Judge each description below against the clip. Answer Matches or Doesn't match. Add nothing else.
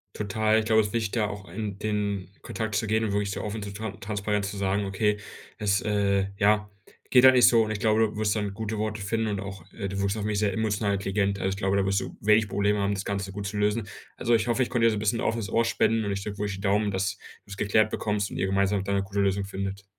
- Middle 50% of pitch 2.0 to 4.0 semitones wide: Doesn't match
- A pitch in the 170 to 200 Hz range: Doesn't match